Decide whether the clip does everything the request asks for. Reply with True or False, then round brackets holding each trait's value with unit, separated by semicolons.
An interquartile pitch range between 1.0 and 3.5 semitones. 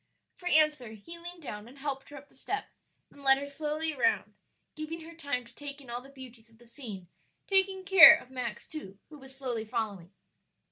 False (4.7 semitones)